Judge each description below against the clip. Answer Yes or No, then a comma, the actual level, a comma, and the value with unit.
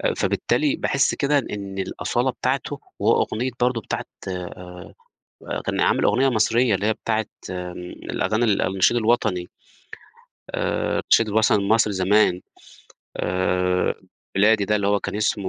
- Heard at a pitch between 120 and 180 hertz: No, low, 105 Hz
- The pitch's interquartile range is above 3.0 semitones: Yes, average, 3.6 semitones